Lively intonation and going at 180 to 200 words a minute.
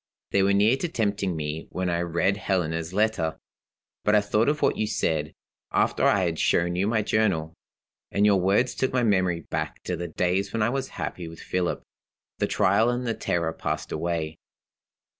No: average, 4.0 semitones; average, 190 wpm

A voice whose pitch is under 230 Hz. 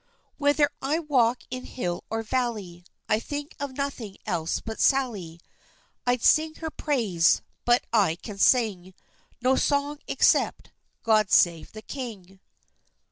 No: high, 235 Hz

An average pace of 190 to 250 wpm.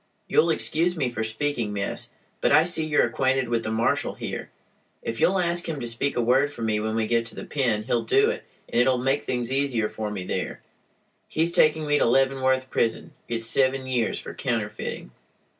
Yes: fast, 205 wpm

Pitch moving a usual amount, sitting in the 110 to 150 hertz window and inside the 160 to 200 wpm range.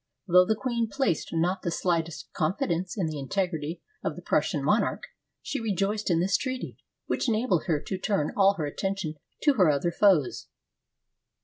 No: average, 4.0 semitones; medium, 185 Hz; average, 180 wpm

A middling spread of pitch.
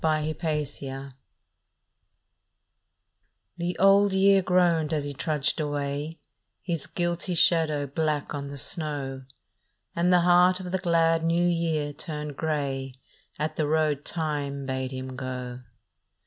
Yes: average, 3.3 semitones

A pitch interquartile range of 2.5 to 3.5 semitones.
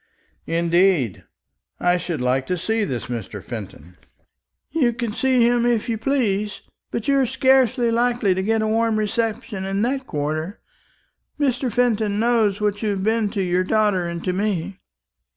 No: average, 4.7 semitones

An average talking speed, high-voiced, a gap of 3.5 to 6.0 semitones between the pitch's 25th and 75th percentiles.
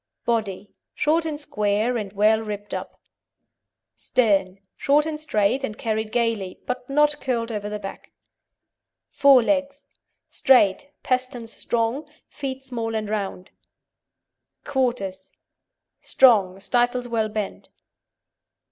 No: slow, 110 wpm; high, 230 Hz; average, 4.2 semitones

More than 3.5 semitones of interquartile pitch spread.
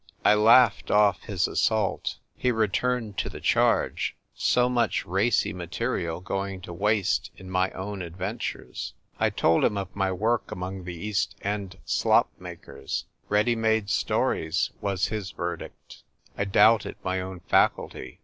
No: average, 2.9 semitones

